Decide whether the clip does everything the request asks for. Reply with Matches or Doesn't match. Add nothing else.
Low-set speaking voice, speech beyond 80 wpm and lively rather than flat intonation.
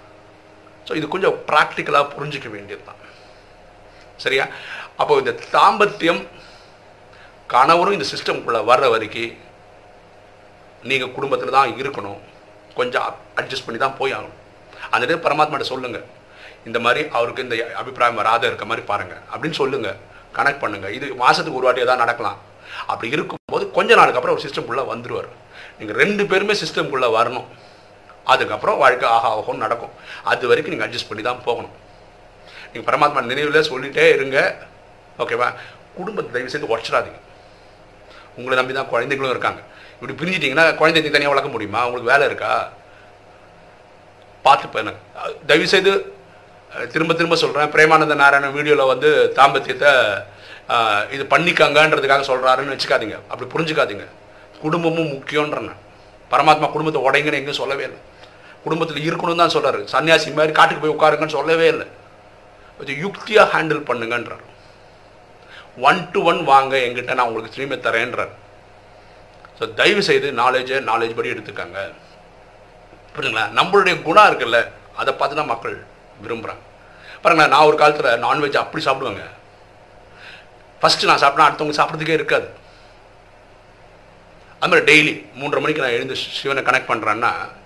Matches